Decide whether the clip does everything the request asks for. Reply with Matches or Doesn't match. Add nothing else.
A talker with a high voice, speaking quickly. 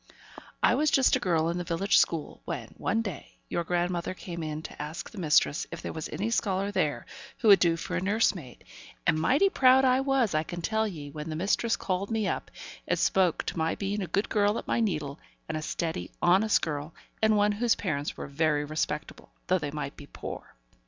Doesn't match